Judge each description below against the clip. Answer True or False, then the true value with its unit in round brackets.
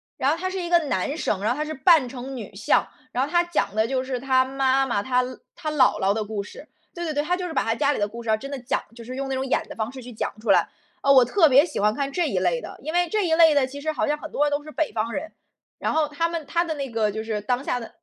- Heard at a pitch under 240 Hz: False (270 Hz)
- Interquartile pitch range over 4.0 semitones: True (5.1 semitones)